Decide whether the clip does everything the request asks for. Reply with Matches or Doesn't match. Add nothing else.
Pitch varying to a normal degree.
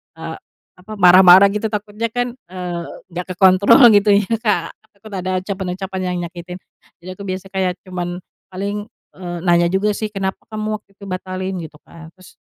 Doesn't match